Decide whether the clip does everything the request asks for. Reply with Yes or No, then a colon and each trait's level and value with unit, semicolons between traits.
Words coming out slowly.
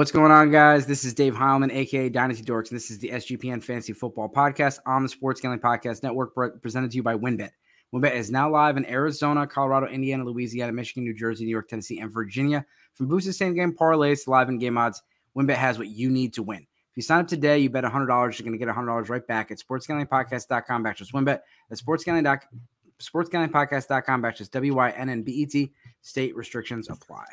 No: average, 195 wpm